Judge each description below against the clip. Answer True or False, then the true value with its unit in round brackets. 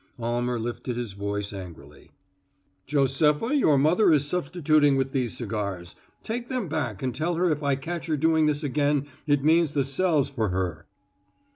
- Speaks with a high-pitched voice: False (140 Hz)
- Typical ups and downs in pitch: True (4.9 semitones)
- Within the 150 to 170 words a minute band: True (165 wpm)